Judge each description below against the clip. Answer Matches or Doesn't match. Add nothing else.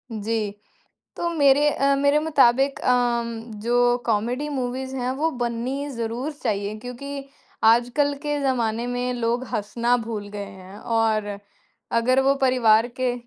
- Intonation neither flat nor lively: Matches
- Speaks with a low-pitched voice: Doesn't match